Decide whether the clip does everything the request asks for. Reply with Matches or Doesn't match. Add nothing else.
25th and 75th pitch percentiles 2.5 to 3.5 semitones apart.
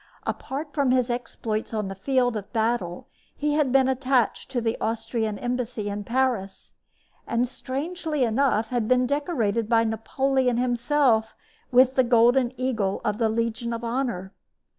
Matches